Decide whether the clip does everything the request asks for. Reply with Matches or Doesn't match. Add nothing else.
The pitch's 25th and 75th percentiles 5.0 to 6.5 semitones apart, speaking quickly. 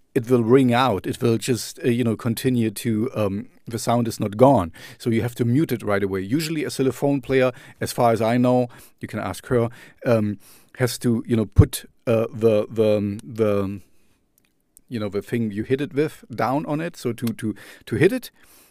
Doesn't match